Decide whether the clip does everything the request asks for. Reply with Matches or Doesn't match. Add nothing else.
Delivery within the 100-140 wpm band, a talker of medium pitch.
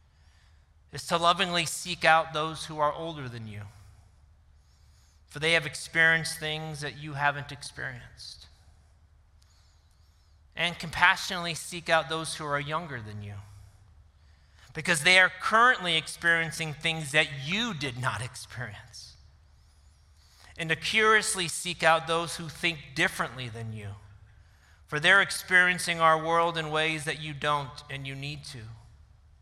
Matches